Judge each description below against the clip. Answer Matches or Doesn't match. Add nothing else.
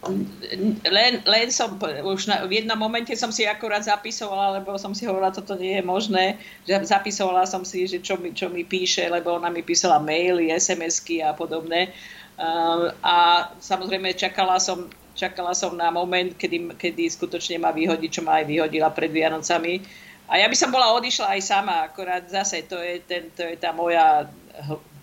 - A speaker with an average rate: Doesn't match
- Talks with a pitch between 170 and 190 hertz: Matches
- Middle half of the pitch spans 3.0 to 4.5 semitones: Doesn't match